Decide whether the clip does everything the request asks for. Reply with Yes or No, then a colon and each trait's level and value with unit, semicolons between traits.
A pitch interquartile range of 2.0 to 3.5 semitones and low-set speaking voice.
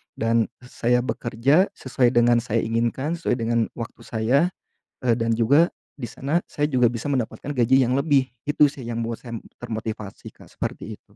Yes: average, 2.9 semitones; low, 120 Hz